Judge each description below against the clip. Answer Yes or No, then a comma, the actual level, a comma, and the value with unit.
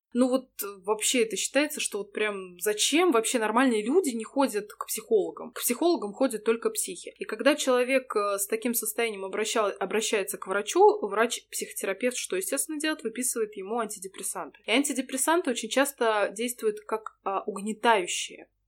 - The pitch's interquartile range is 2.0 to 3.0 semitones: No, average, 4.2 semitones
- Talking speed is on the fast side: No, average, 145 wpm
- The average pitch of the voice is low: No, high, 230 Hz